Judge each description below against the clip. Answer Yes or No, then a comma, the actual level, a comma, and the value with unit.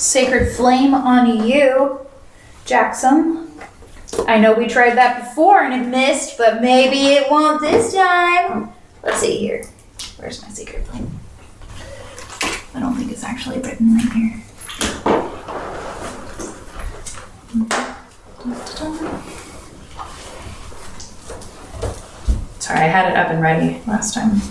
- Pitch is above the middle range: Yes, very high, 255 Hz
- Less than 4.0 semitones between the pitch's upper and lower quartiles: Yes, average, 3.6 semitones